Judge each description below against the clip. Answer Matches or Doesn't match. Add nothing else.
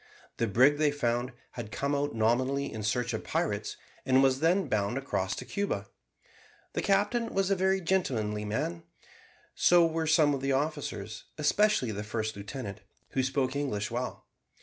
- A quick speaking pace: Doesn't match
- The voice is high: Doesn't match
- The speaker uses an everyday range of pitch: Doesn't match